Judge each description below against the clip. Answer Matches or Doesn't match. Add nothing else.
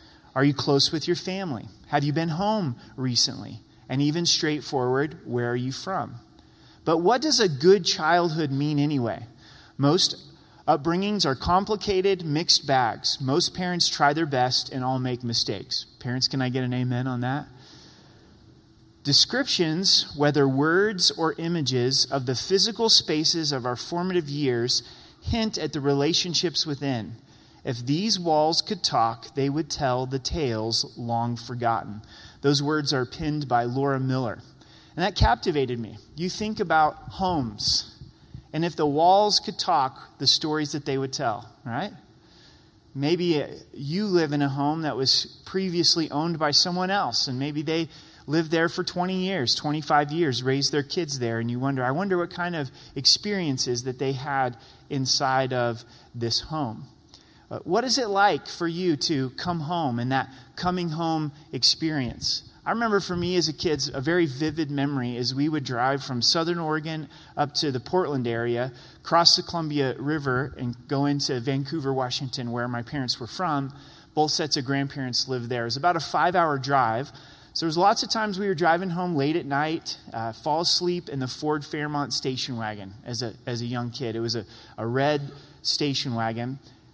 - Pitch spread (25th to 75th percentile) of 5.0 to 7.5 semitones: Doesn't match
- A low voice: Doesn't match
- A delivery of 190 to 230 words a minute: Doesn't match